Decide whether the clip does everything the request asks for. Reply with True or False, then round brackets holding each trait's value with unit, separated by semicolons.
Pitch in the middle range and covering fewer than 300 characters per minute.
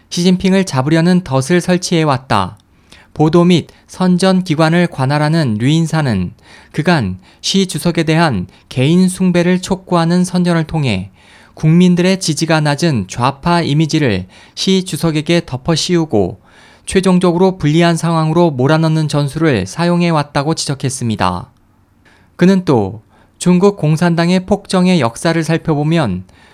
True (160 Hz; 290 characters per minute)